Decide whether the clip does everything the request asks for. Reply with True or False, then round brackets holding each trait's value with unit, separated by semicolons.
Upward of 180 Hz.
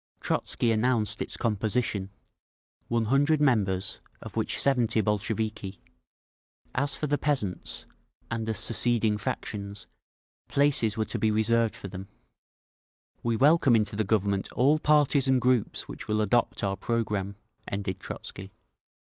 False (110 Hz)